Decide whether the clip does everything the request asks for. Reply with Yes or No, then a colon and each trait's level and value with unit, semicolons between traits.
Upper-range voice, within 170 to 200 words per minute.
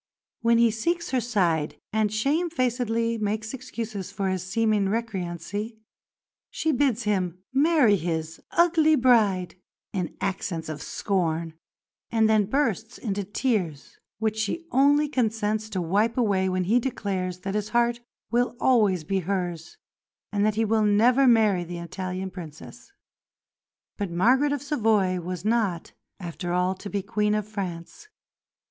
No: high, 210 Hz; average, 140 wpm